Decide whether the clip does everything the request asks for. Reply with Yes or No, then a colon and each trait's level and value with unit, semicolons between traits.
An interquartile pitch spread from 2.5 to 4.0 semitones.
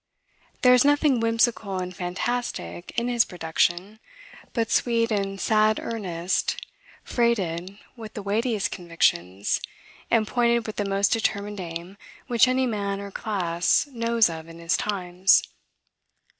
No: average, 4.5 semitones